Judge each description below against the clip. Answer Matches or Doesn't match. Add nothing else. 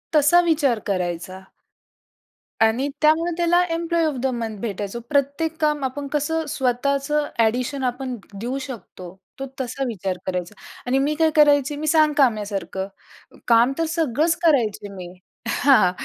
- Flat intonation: Doesn't match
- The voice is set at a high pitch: Matches